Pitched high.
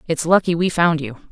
No: medium, 165 Hz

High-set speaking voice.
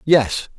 No: low, 135 Hz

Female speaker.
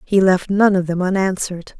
Yes: female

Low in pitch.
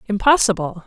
No: high, 205 Hz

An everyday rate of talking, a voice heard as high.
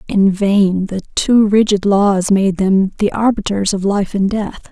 Yes: average, 180 wpm; high, 200 Hz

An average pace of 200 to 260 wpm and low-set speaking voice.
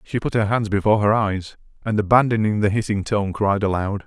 Yes: fast, 205 wpm; low, 105 Hz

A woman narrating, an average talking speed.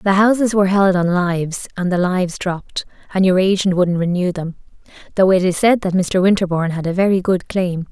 No: female; fast, 210 wpm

